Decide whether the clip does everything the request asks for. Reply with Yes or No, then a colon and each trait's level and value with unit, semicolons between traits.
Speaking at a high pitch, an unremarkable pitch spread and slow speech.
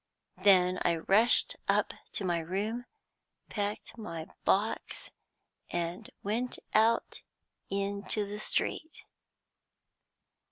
Yes: high, 200 Hz; average, 3.2 semitones; slow, 90 wpm